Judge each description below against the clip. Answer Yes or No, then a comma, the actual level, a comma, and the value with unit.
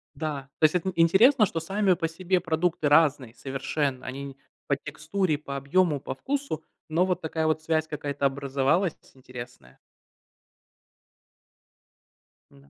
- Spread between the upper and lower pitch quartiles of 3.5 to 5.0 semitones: Yes, average, 4.2 semitones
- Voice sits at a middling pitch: Yes, medium, 155 Hz